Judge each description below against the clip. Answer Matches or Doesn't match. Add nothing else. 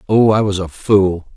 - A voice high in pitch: Doesn't match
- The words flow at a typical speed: Doesn't match